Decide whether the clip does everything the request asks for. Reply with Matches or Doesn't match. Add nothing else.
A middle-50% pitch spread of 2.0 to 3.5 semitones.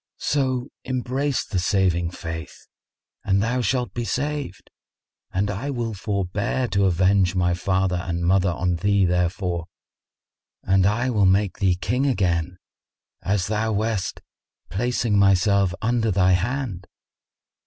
Doesn't match